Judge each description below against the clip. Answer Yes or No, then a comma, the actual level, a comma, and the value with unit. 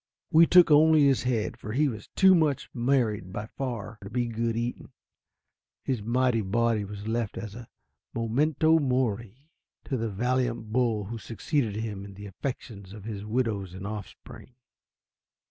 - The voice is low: Yes, low, 115 Hz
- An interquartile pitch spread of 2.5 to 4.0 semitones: Yes, average, 3.5 semitones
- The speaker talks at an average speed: Yes, average, 160 wpm